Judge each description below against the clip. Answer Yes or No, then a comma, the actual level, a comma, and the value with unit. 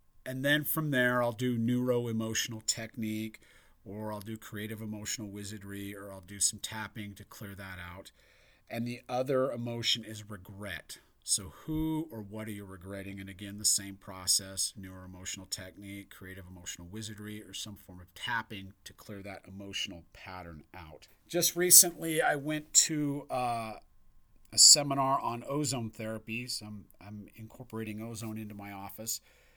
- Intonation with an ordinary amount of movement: Yes, average, 3.2 semitones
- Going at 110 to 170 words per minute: Yes, average, 160 wpm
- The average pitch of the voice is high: No, low, 105 Hz